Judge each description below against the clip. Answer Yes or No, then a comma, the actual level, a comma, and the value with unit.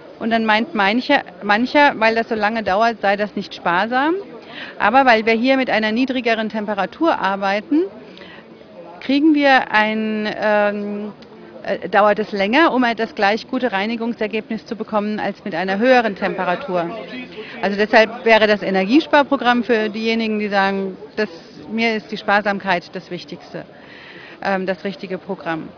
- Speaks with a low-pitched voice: No, high, 215 Hz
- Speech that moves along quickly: No, average, 150 wpm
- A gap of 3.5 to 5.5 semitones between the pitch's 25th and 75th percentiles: No, average, 2.9 semitones